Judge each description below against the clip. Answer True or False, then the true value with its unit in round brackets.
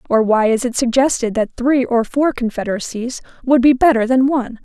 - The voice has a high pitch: True (245 Hz)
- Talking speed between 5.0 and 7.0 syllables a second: True (5.5 syllables/s)